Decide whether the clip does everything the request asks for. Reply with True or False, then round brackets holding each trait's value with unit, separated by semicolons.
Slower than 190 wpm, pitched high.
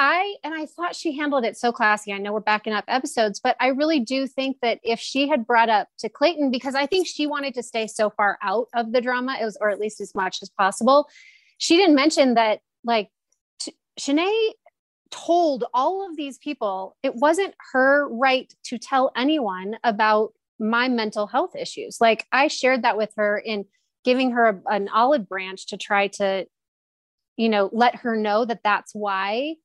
False (200 wpm; 240 Hz)